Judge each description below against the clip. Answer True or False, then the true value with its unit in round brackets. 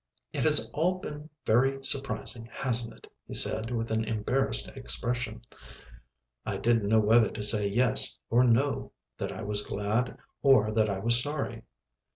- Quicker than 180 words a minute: False (160 wpm)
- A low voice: True (115 Hz)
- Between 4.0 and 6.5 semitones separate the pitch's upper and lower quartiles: False (3.1 semitones)